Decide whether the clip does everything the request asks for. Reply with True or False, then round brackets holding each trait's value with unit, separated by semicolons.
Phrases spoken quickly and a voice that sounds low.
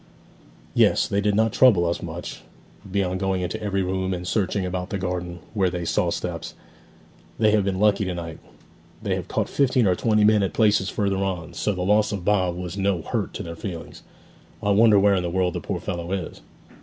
True (210 wpm; 95 Hz)